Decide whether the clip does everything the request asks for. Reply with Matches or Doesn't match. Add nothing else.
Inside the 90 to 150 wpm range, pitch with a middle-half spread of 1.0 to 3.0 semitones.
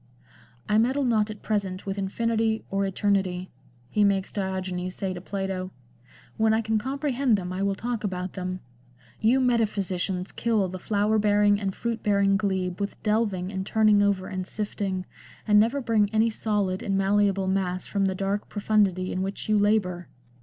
Doesn't match